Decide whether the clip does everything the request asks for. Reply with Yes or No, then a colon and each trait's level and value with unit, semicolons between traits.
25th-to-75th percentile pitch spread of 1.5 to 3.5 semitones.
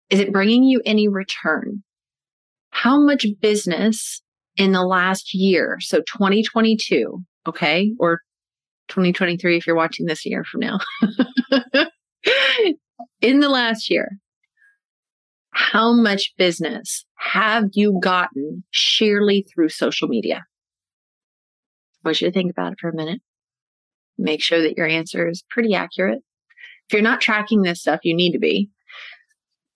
No: average, 4.6 semitones